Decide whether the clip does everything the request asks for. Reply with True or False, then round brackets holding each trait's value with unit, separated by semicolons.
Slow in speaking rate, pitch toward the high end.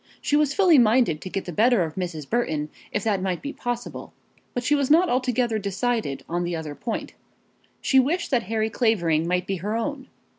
False (200 wpm; 220 Hz)